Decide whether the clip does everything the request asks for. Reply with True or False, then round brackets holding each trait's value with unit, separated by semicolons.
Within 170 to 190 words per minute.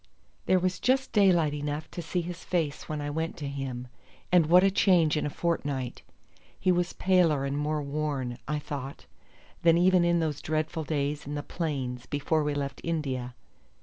True (180 wpm)